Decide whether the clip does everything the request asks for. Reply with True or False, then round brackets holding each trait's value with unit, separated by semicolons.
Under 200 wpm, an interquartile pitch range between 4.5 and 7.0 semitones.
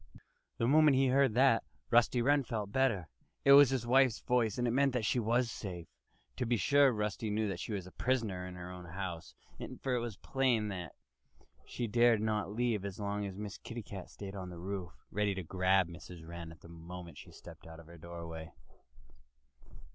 False (205 wpm; 5.2 semitones)